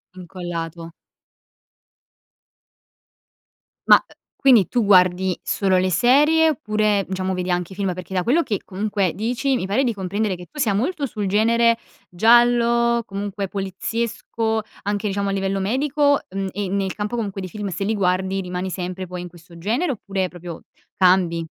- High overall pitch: Yes, high, 195 Hz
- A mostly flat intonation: No, average, 3.8 semitones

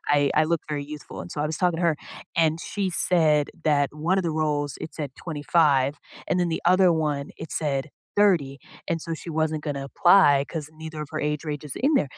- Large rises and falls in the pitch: No, narrow, 2.6 semitones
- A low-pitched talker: No, medium, 155 Hz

